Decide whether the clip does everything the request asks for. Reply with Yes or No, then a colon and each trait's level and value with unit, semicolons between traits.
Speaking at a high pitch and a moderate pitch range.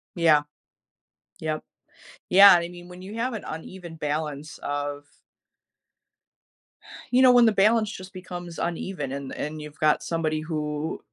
No: medium, 165 Hz; average, 3.8 semitones